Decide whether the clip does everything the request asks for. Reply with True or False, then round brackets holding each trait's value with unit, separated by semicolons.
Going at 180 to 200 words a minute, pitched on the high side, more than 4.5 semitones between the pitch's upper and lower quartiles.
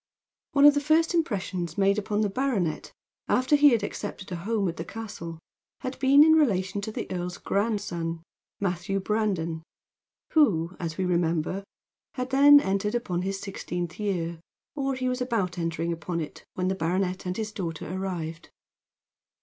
False (165 wpm; 195 Hz; 5.5 semitones)